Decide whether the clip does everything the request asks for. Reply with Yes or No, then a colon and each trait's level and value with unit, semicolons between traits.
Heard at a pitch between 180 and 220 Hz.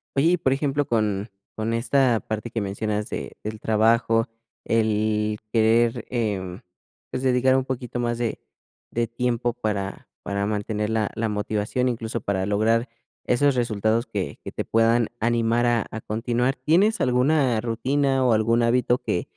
No: low, 115 Hz